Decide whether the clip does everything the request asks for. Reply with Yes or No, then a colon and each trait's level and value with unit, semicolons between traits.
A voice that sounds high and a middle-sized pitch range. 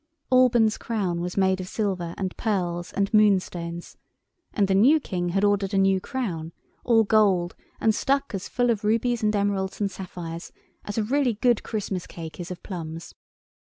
Yes: high, 200 Hz; average, 3.6 semitones